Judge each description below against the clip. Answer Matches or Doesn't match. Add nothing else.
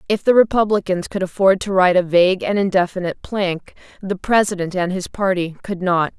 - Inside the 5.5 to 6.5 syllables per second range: Matches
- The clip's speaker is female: Matches